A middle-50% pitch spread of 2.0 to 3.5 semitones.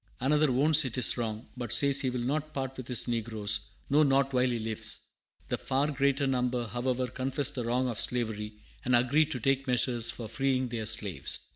Yes: narrow, 2.5 semitones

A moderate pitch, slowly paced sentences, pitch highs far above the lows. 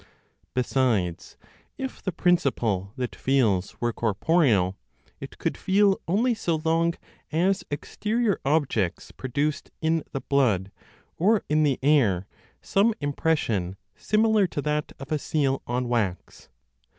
Yes: medium, 145 Hz; slow, 125 wpm; wide, 6.5 semitones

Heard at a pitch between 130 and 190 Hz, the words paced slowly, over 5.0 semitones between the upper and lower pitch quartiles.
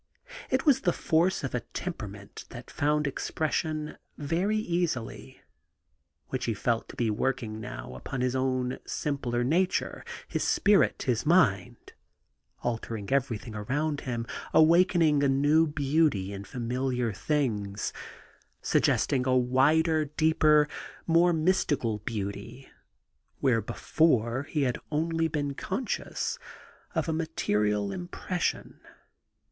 Yes: medium, 140 Hz; slow, 120 wpm; wide, 5.6 semitones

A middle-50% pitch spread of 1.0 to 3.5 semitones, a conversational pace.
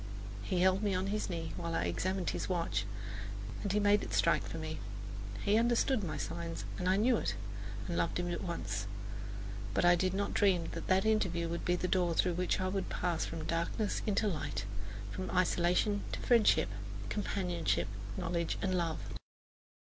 Yes: average, 2.8 semitones; average, 180 wpm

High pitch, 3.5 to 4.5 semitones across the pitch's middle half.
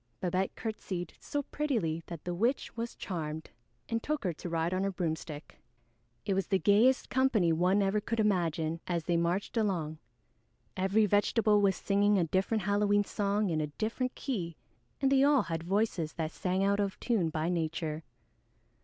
Yes: high, 195 Hz; average, 4.2 semitones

